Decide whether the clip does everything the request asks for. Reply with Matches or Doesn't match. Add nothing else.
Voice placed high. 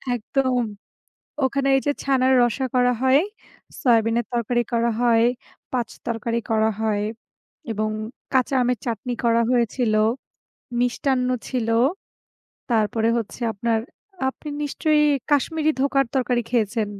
Matches